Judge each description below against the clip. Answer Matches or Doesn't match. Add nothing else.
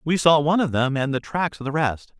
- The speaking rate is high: Matches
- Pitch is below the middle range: Doesn't match